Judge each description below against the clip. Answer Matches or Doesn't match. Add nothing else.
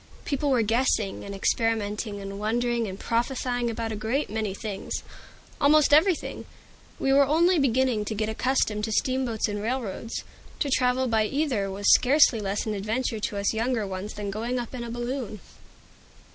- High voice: Matches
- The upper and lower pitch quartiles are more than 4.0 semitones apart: Doesn't match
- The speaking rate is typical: Matches